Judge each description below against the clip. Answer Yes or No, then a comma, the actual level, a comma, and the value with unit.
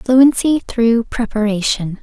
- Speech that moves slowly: Yes, slow, 90 wpm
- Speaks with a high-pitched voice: Yes, high, 230 Hz